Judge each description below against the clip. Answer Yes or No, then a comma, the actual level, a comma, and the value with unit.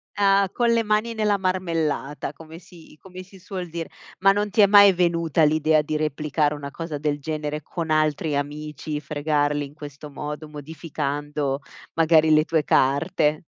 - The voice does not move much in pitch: No, average, 3.5 semitones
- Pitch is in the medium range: Yes, medium, 155 Hz